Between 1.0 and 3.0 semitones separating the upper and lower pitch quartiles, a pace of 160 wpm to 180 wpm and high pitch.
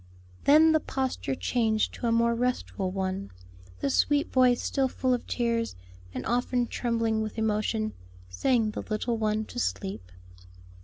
No: narrow, 2.6 semitones; average, 150 wpm; high, 230 Hz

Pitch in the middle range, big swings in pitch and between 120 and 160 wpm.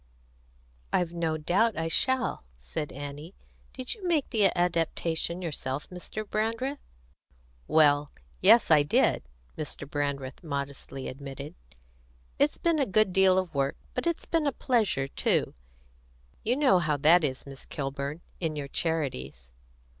Yes: medium, 165 Hz; wide, 7.1 semitones; average, 140 wpm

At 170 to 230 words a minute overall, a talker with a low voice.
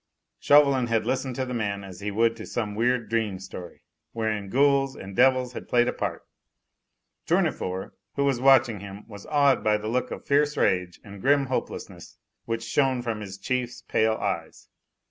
Yes: average, 180 wpm; low, 115 Hz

